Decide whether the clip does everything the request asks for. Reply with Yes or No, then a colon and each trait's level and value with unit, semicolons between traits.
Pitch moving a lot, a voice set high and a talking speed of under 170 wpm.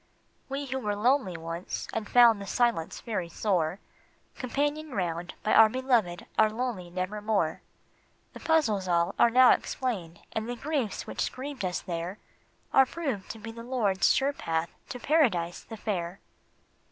Yes: wide, 6.0 semitones; high, 215 Hz; average, 160 wpm